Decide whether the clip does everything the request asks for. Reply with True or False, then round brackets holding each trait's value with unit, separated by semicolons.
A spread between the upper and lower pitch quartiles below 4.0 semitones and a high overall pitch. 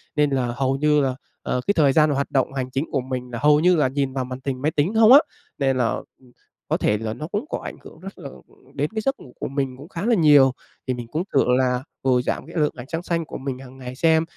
False (3.5 semitones; 140 Hz)